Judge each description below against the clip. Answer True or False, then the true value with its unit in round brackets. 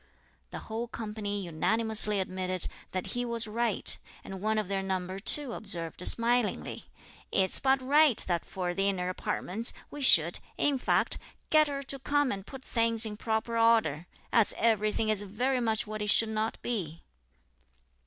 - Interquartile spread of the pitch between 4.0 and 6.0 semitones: False (3.6 semitones)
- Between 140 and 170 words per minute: True (165 wpm)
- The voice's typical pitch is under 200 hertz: False (215 Hz)